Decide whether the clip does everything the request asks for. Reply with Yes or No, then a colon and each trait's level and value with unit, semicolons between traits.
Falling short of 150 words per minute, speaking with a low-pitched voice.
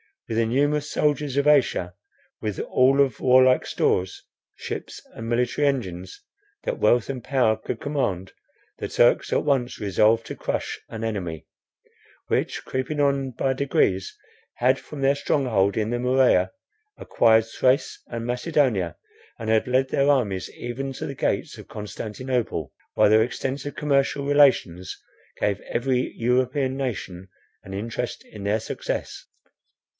Yes: average, 140 wpm; low, 125 Hz